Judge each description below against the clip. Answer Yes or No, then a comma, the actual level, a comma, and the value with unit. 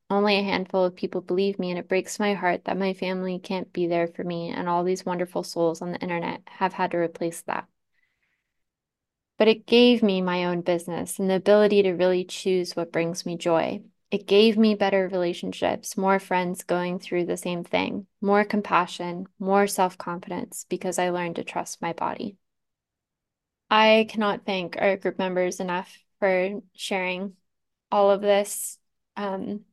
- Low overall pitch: No, medium, 185 Hz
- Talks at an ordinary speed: Yes, average, 175 wpm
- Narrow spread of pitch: Yes, narrow, 2.2 semitones